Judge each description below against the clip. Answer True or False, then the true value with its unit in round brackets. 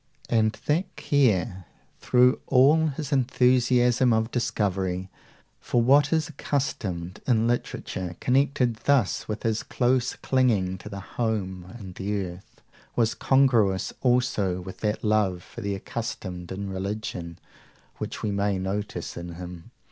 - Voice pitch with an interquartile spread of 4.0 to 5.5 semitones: True (5.1 semitones)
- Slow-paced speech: True (130 wpm)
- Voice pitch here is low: True (110 Hz)